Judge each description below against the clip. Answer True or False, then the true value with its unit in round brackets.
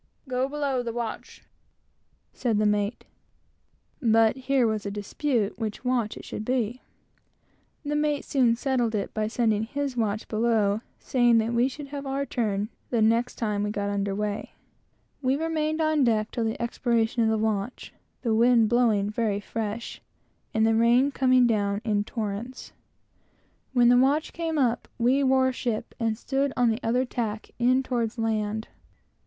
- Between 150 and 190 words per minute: True (165 wpm)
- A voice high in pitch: True (235 Hz)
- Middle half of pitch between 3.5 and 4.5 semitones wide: False (3.0 semitones)